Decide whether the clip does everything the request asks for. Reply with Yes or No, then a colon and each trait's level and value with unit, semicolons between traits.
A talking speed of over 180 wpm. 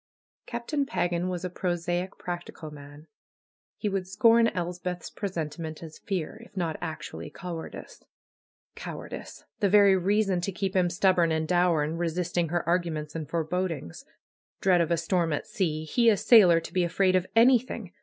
No: average, 160 wpm